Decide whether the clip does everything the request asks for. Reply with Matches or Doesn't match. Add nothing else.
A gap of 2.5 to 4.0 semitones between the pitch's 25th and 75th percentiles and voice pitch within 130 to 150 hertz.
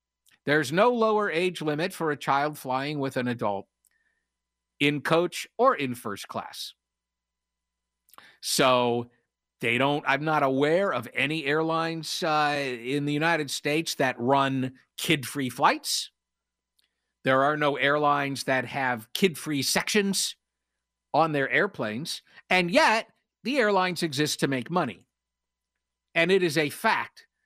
Doesn't match